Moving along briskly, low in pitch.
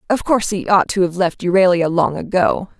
No: fast, 215 wpm; medium, 185 Hz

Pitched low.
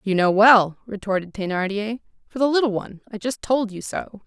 No: high, 215 Hz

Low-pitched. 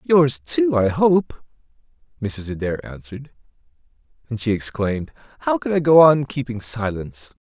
Yes: low, 120 Hz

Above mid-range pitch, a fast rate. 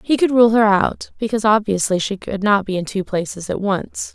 Yes: high, 205 Hz; fast, 230 wpm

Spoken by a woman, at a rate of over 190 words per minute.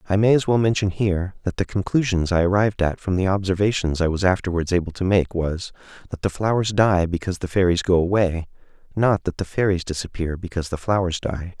No: male; fast, 205 wpm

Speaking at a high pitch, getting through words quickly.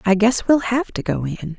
Yes: high, 215 Hz; fast, 265 wpm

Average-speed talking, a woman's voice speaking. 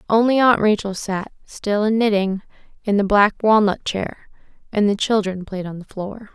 Yes: average, 180 wpm; female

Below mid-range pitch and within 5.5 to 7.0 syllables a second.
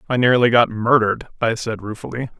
Yes: low, 115 Hz; 6.0 syllables/s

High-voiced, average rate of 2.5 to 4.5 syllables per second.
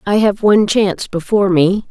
No: high, 200 Hz; 5.8 syllables/s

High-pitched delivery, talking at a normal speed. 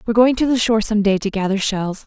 No: high, 215 Hz; fast, 290 wpm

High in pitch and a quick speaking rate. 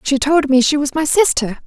Yes: very high, 285 Hz; fast, 255 wpm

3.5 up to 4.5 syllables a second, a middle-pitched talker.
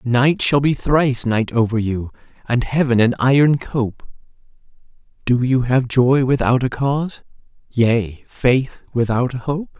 No: 4.2 syllables/s; low, 125 Hz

